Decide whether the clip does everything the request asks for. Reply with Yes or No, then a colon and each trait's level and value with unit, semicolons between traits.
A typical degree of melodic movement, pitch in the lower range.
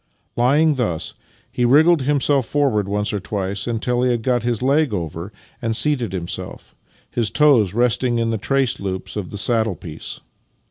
Yes: average, 4.5 semitones; low, 120 Hz